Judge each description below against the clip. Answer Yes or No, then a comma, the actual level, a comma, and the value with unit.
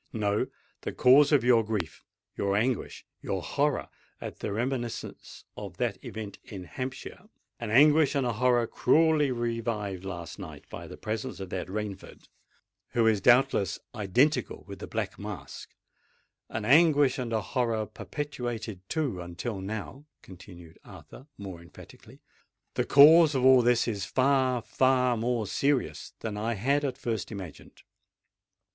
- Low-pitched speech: Yes, low, 115 Hz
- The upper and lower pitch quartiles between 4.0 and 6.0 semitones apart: Yes, average, 4.5 semitones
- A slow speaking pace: Yes, slow, 130 wpm